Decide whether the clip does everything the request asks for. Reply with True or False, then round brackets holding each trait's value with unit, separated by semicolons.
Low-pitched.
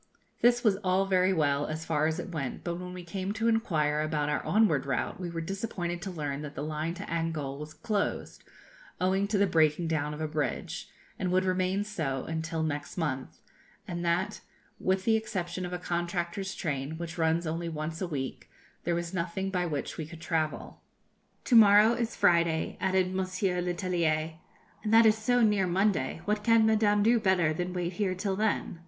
False (175 Hz)